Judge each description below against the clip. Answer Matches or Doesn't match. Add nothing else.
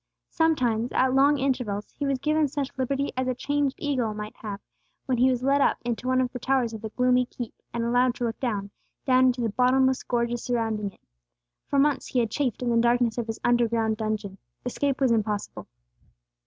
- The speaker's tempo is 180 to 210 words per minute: Matches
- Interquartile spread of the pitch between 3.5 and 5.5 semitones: Doesn't match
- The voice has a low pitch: Doesn't match